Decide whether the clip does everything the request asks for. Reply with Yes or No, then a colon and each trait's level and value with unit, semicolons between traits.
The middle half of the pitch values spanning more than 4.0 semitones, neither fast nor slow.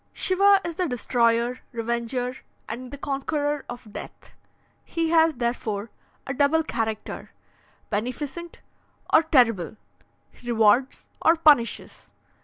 No: average, 5.2 semitones; slow, 110 wpm